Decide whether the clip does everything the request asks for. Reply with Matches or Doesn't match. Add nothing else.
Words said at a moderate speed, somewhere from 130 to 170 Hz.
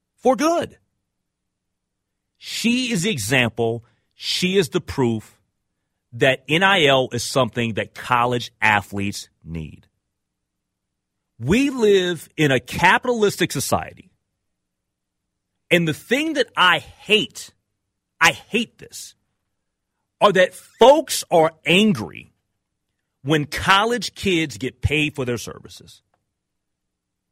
Doesn't match